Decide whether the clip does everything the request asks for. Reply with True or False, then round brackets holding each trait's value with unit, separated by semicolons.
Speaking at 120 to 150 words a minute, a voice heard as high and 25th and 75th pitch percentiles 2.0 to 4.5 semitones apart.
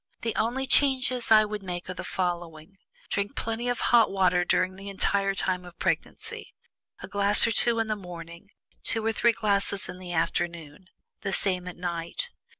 False (180 wpm; 195 Hz; 3.9 semitones)